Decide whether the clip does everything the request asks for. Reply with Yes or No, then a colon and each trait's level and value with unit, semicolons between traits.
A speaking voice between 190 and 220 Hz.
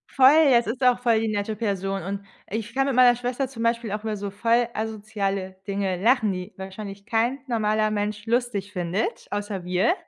Yes: high, 215 Hz